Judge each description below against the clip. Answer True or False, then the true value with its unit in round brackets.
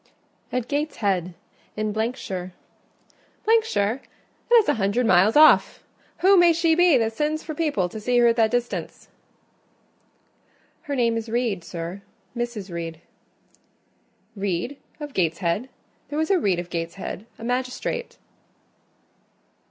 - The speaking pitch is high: True (230 Hz)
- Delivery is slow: True (130 wpm)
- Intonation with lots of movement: True (7.2 semitones)